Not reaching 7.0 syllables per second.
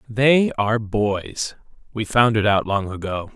Yes: 4.0 syllables/s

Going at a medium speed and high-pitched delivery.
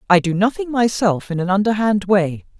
Yes: average, 185 wpm; high, 200 Hz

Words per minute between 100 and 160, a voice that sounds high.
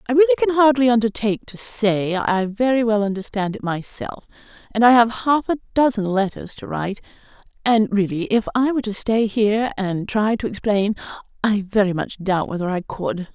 No: average, 185 wpm; high, 220 Hz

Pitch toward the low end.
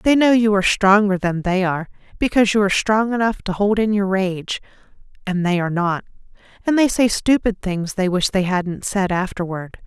No: high, 200 Hz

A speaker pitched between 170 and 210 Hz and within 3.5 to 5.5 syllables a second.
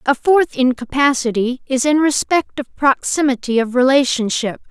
No: very high, 265 Hz; 4.7 syllables/s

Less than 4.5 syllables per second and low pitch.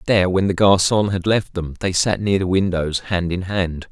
No: 4.9 syllables/s; very low, 95 Hz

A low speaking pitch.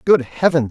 No: medium, 150 Hz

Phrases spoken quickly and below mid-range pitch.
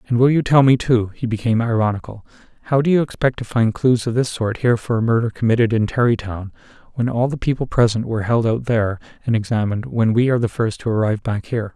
Yes: fast, 225 wpm; low, 115 Hz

